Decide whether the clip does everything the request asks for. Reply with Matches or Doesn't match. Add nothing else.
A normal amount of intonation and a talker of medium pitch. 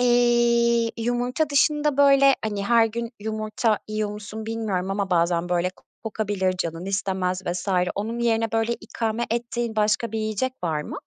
Doesn't match